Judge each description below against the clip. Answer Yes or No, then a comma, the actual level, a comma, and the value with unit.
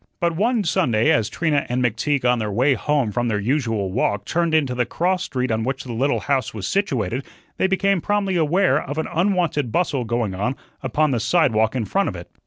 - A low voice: Yes, low, 130 Hz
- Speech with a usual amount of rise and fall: No, wide, 6.7 semitones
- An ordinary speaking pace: No, fast, 210 wpm